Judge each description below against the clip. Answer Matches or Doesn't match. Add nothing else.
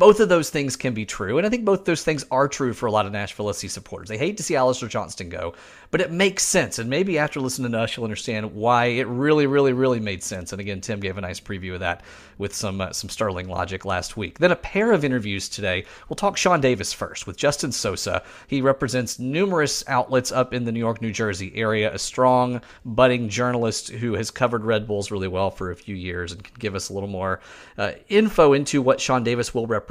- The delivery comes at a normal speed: Doesn't match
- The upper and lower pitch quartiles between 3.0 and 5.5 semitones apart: Matches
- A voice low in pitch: Matches